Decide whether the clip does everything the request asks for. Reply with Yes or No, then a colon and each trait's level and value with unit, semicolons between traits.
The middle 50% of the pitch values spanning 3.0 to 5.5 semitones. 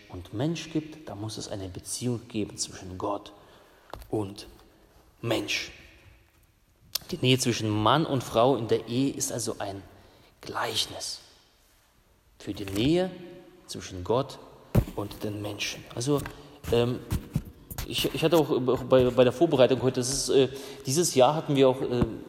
Yes: average, 5.1 semitones